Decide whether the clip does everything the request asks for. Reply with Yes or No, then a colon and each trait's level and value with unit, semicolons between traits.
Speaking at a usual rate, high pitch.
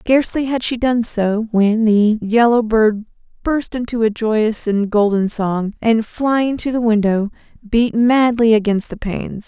Yes: average, 165 wpm; high, 225 Hz